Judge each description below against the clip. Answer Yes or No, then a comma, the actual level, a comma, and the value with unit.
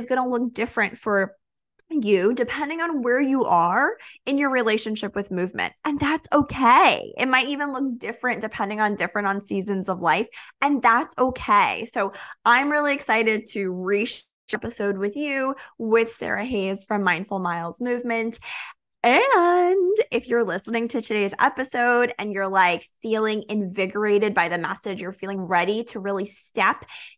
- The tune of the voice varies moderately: Yes, average, 4.3 semitones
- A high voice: Yes, high, 225 Hz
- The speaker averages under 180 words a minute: Yes, average, 160 wpm